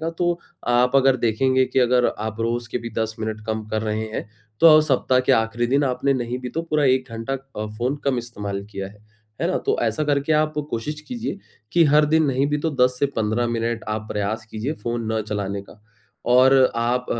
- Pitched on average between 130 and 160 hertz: No, low, 120 Hz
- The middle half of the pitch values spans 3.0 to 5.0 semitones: Yes, average, 3.6 semitones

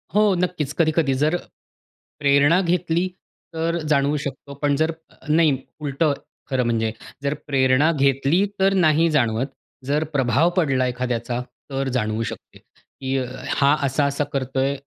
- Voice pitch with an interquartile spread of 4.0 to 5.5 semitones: No, average, 3.2 semitones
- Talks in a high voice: No, medium, 140 Hz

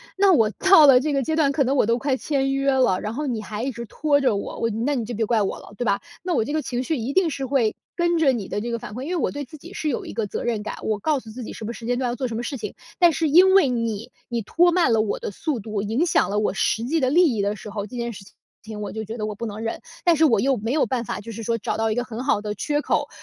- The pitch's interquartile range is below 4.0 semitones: No, average, 4.8 semitones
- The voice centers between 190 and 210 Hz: No, high, 245 Hz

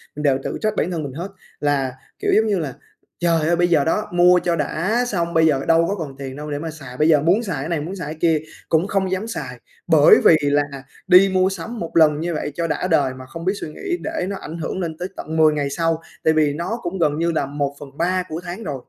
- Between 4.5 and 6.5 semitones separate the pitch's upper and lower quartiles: No, average, 3.6 semitones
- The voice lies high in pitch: No, medium, 165 Hz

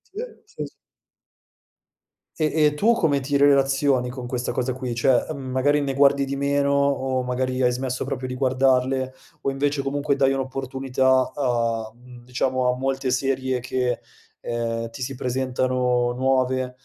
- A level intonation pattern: Yes, narrow, 1.5 semitones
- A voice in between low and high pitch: No, low, 130 Hz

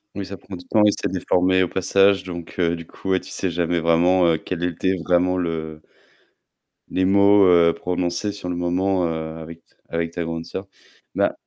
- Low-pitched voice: Yes, very low, 90 Hz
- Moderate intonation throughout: No, narrow, 2.0 semitones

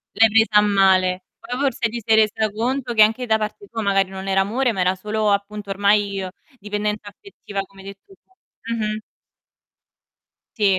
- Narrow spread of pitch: Yes, narrow, 2.2 semitones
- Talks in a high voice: Yes, high, 210 Hz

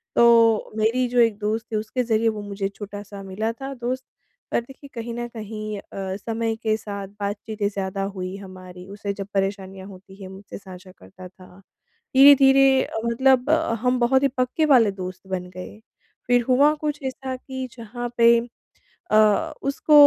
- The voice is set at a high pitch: Yes, high, 220 Hz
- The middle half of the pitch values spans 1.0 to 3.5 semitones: No, average, 4.3 semitones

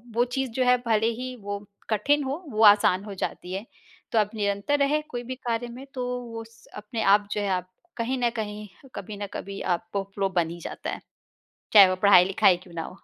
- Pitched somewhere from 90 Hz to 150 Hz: No, high, 215 Hz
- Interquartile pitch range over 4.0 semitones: No, average, 3.4 semitones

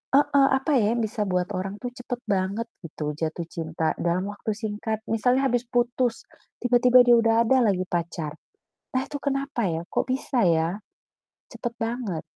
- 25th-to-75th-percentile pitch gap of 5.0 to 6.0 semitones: Yes, average, 5.3 semitones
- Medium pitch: No, high, 225 Hz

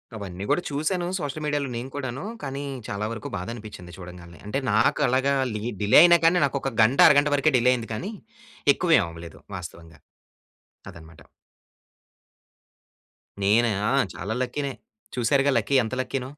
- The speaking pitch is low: Yes, low, 120 Hz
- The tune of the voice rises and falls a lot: Yes, wide, 5.9 semitones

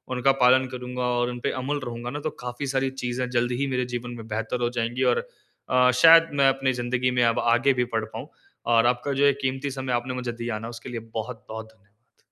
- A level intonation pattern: Yes, narrow, 1.8 semitones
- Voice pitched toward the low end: Yes, low, 125 Hz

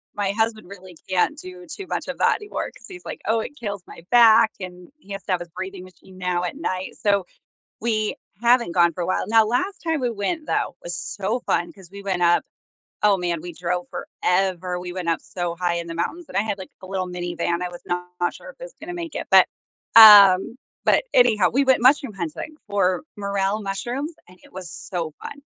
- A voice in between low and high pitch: No, high, 195 Hz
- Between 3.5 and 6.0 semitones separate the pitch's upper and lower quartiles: Yes, average, 4.6 semitones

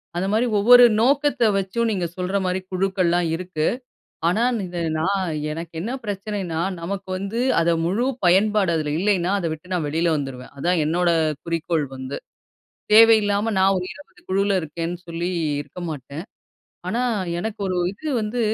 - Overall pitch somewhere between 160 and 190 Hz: Yes, medium, 185 Hz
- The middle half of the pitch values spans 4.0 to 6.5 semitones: No, average, 3.5 semitones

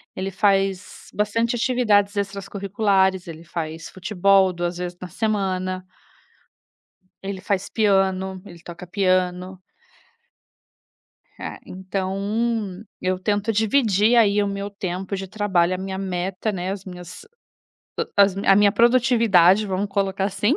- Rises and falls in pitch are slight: Yes, narrow, 1.8 semitones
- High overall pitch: Yes, high, 195 Hz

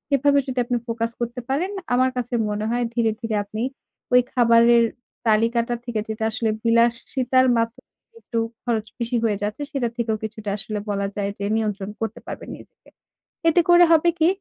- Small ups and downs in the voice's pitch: Yes, narrow, 2.3 semitones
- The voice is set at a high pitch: Yes, high, 235 Hz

